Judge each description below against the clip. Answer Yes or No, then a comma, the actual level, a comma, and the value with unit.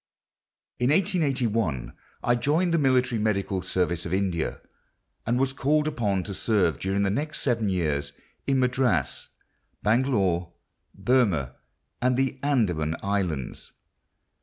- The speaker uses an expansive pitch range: Yes, wide, 6.3 semitones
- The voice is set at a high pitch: No, low, 110 Hz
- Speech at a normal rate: No, slow, 120 wpm